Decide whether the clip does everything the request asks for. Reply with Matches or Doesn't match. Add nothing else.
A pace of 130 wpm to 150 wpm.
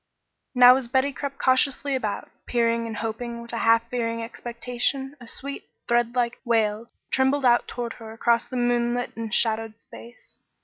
Doesn't match